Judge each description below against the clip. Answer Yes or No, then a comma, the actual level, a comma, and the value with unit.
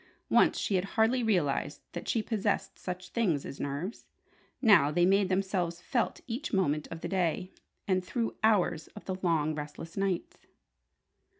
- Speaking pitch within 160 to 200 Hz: Yes, medium, 185 Hz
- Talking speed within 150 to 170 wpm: Yes, average, 160 wpm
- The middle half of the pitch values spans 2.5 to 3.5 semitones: No, average, 4.2 semitones